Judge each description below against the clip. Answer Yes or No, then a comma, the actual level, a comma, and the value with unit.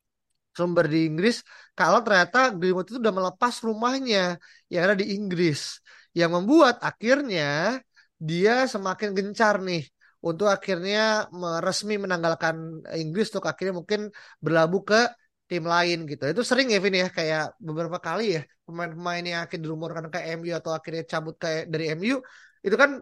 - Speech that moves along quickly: Yes, fast, 150 wpm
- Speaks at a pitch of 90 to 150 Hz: No, medium, 180 Hz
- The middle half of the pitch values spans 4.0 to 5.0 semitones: Yes, average, 4.3 semitones